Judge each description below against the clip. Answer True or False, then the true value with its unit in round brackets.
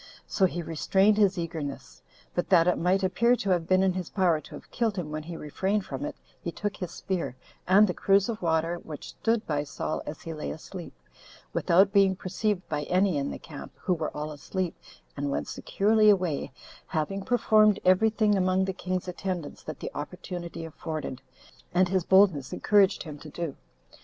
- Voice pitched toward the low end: False (180 Hz)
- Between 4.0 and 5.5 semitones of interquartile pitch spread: False (3.4 semitones)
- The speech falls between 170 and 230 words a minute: True (190 wpm)